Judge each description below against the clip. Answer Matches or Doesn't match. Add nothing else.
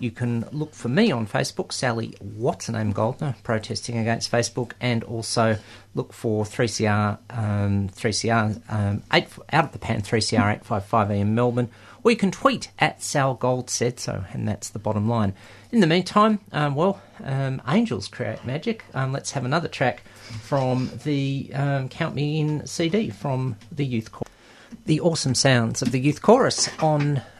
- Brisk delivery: Doesn't match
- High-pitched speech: Doesn't match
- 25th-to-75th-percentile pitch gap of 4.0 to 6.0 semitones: Matches